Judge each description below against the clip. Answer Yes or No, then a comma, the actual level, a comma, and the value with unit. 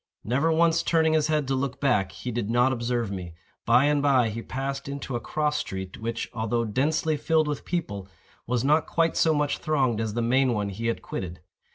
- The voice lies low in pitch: Yes, low, 130 Hz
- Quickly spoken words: Yes, fast, 210 wpm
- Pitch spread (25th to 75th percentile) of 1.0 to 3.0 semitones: No, average, 4.5 semitones